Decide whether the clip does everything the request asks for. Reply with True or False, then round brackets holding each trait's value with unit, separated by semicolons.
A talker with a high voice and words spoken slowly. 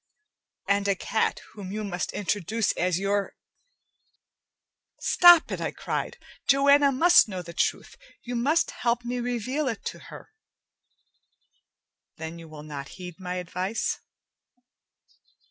True (205 Hz; 130 wpm)